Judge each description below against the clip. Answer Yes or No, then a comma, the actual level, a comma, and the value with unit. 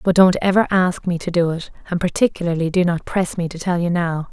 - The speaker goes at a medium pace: No, fast, 250 wpm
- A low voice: No, medium, 175 Hz